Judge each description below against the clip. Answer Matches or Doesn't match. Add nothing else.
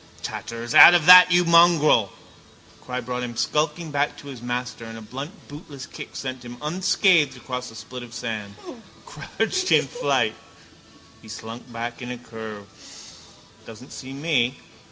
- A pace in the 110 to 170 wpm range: Matches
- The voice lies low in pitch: Matches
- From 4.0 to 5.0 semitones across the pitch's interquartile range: Matches